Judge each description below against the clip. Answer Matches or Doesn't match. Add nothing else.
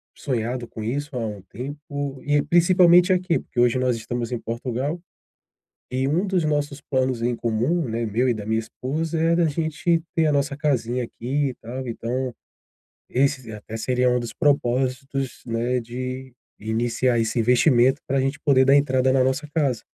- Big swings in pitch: Doesn't match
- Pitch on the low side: Matches